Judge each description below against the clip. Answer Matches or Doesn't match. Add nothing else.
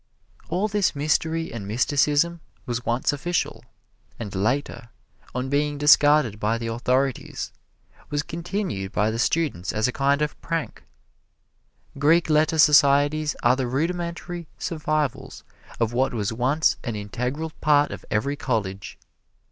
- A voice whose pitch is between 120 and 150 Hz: Matches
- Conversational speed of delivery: Doesn't match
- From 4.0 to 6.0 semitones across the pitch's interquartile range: Matches